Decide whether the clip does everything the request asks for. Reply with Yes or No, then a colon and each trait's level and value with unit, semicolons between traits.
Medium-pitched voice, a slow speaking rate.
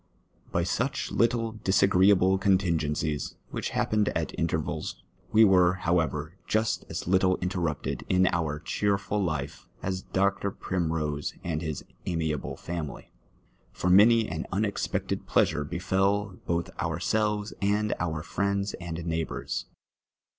No: very low, 90 Hz; slow, 120 wpm